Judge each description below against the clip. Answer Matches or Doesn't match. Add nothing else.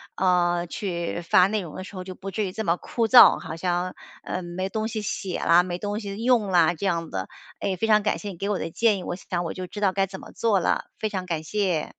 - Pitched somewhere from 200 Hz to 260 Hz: Doesn't match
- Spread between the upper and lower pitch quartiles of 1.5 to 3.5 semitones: Matches